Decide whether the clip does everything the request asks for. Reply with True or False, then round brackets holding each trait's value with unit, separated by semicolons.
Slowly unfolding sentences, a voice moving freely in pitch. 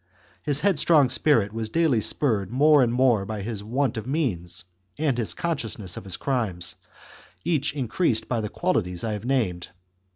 False (165 wpm; 5.7 semitones)